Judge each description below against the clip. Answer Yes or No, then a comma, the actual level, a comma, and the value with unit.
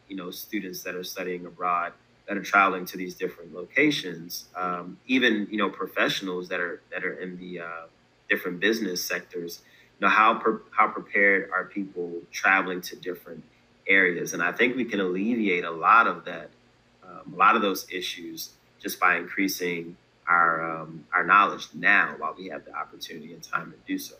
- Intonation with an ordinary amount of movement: No, narrow, 1.8 semitones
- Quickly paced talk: No, average, 185 wpm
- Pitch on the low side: Yes, very low, 90 Hz